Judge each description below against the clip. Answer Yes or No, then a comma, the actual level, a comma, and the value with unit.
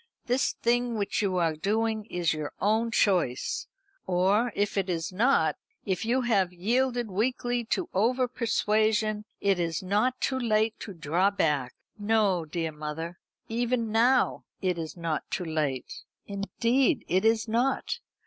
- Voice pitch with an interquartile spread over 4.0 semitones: Yes, average, 4.9 semitones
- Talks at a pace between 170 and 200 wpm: No, average, 150 wpm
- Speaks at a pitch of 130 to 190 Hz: No, high, 210 Hz